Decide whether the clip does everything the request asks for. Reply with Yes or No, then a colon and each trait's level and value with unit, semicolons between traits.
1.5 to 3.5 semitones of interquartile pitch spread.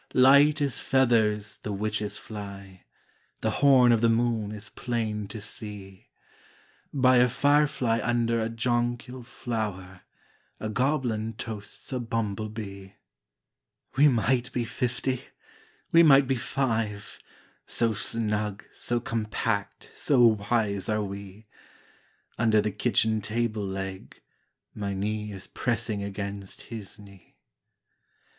Yes: average, 2.8 semitones